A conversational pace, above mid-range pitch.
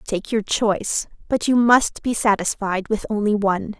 Yes: average, 175 wpm; high, 210 Hz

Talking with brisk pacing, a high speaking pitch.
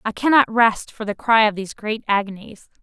Yes: fast, 210 wpm; high, 220 Hz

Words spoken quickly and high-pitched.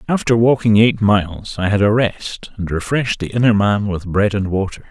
No: fast, 210 wpm; low, 105 Hz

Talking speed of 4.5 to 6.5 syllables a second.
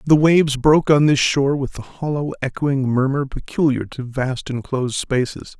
Yes: 5.1 syllables/s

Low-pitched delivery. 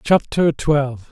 No: medium, 150 Hz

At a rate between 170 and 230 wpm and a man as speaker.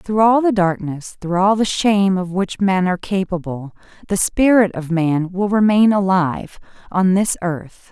No: average, 175 wpm; female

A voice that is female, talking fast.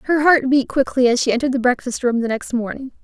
Yes: female; fast, 255 wpm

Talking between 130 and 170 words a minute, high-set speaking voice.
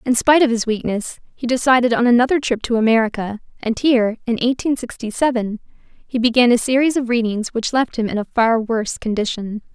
No: average, 195 wpm; high, 235 Hz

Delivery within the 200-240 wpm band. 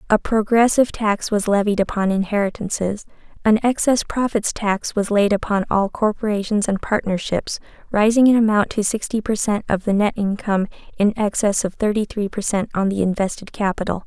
No: average, 170 wpm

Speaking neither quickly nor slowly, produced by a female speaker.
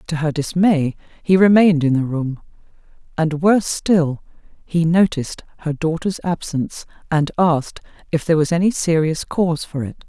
Yes: average, 155 wpm; female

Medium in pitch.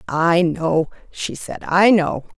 Yes: medium, 170 Hz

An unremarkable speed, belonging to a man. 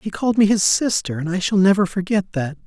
No: fast, 245 wpm; male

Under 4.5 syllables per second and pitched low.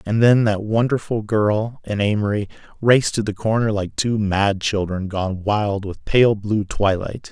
Yes: 4.2 syllables/s; low, 105 Hz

